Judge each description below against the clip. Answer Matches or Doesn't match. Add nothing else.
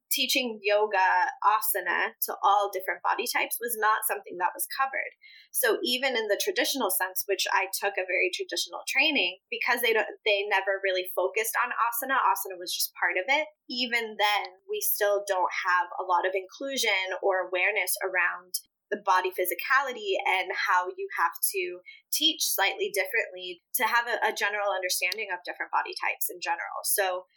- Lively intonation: Matches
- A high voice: Matches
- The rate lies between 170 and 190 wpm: Matches